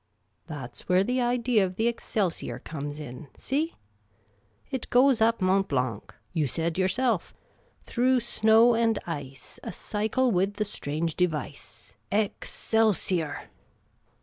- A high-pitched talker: Yes, high, 195 Hz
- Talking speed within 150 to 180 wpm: No, slow, 135 wpm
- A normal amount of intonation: No, wide, 7.1 semitones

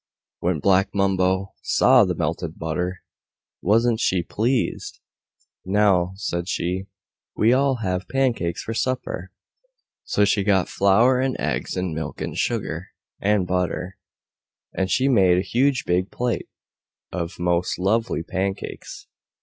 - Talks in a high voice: No, very low, 95 Hz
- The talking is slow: Yes, slow, 130 wpm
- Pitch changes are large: No, average, 4.0 semitones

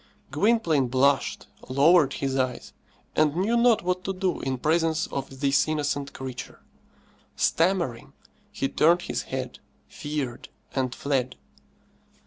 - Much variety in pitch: No, average, 4.5 semitones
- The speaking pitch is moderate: Yes, medium, 145 Hz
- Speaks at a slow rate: Yes, slow, 120 wpm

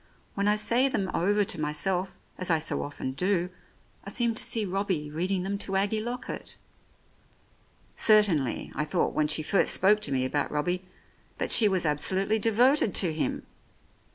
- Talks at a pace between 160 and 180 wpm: Yes, average, 170 wpm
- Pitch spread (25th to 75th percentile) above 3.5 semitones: Yes, average, 5.2 semitones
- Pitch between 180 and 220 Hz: Yes, high, 190 Hz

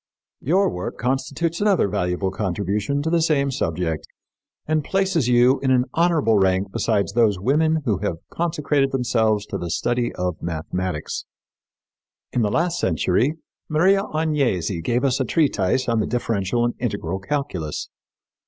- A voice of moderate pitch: No, low, 120 Hz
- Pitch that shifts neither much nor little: No, wide, 7.6 semitones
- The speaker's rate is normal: Yes, average, 145 wpm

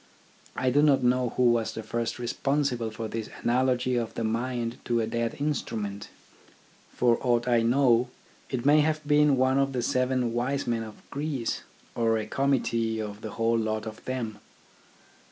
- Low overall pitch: Yes, low, 120 Hz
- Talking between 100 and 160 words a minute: No, average, 170 wpm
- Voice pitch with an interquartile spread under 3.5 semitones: Yes, narrow, 2.4 semitones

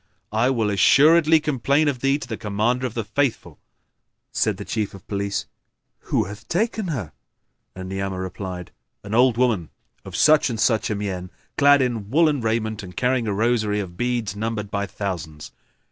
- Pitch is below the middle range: Yes, low, 110 Hz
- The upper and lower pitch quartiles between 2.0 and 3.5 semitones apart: No, average, 4.4 semitones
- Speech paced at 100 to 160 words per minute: No, average, 175 wpm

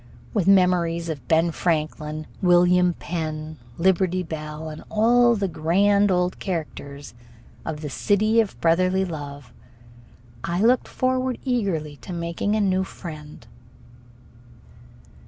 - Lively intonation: No, average, 4.0 semitones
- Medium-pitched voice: Yes, medium, 175 Hz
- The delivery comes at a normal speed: No, slow, 120 wpm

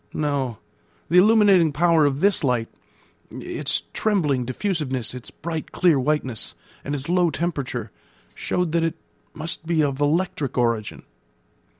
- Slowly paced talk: Yes, slow, 130 wpm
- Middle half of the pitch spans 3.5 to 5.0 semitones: Yes, average, 4.6 semitones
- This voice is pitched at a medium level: Yes, medium, 150 Hz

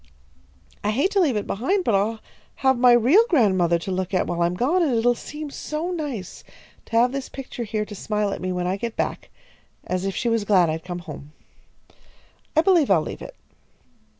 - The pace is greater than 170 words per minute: Yes, fast, 205 wpm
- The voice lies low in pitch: No, high, 220 Hz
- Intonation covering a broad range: Yes, wide, 6.7 semitones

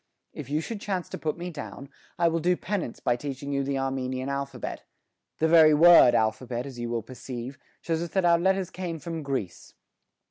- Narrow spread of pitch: No, average, 4.6 semitones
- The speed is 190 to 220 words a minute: Yes, average, 200 wpm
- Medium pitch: Yes, medium, 145 Hz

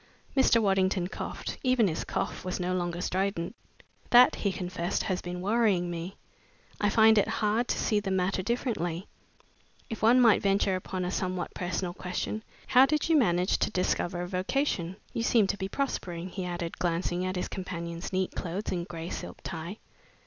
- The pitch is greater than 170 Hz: Yes, medium, 185 Hz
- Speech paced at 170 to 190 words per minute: Yes, average, 180 wpm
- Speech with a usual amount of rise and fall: Yes, average, 3.3 semitones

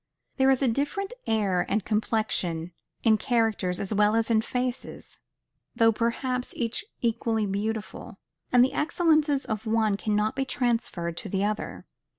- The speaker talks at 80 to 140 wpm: No, average, 150 wpm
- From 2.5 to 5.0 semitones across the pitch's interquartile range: Yes, average, 3.1 semitones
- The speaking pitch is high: Yes, high, 225 Hz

